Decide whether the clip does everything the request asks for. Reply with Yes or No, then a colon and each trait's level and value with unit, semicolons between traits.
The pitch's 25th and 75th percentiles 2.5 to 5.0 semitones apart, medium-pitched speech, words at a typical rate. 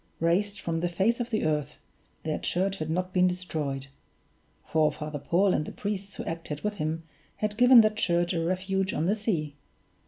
Yes: average, 4.2 semitones; medium, 180 Hz; average, 190 wpm